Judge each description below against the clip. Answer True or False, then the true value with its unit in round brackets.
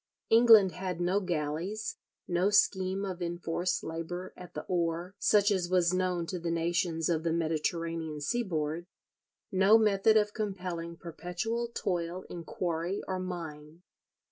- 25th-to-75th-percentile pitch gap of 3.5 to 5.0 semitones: False (2.5 semitones)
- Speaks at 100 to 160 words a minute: True (140 wpm)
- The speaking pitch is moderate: True (175 Hz)